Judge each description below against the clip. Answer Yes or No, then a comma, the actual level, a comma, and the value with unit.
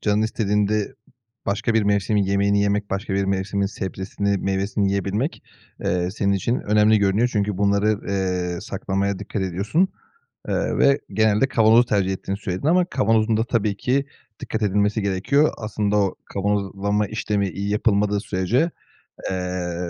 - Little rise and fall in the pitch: Yes, narrow, 1.8 semitones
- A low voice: Yes, low, 100 Hz